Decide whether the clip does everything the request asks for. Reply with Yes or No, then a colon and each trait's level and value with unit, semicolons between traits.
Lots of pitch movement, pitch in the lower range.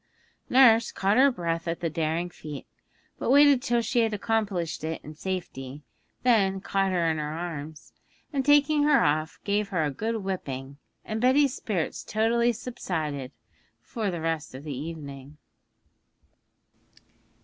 No: wide, 6.8 semitones; medium, 185 Hz